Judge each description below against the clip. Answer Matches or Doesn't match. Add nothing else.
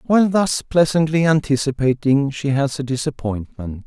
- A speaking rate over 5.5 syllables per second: Doesn't match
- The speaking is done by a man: Matches